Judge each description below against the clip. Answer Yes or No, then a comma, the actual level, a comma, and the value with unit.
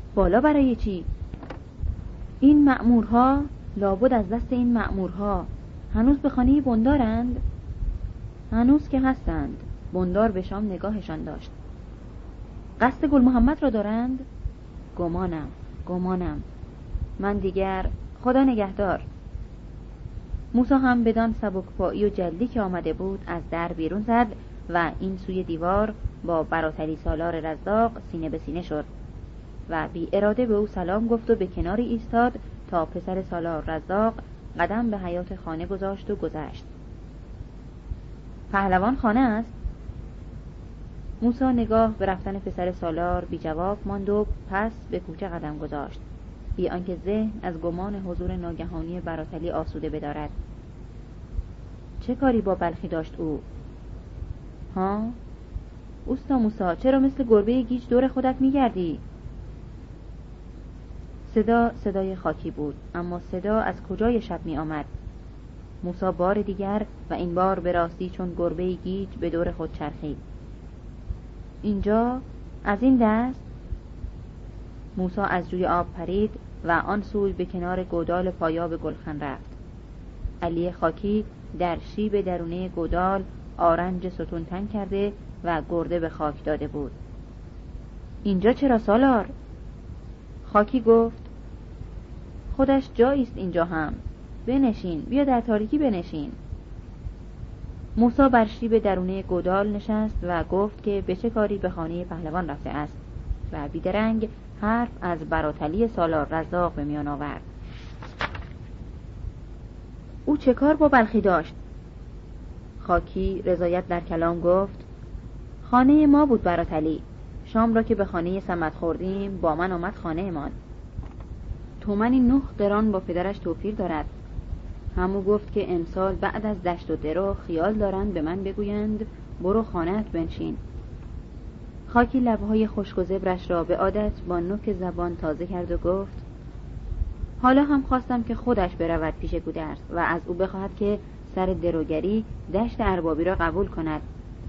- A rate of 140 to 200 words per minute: No, average, 130 wpm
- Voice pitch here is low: No, medium, 185 Hz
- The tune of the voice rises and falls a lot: No, average, 4.6 semitones